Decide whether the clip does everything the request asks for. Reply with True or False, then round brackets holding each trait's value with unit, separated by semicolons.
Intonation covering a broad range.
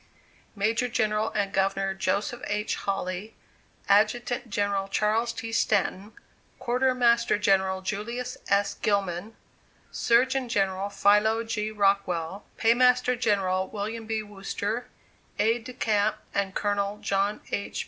False (2.6 semitones)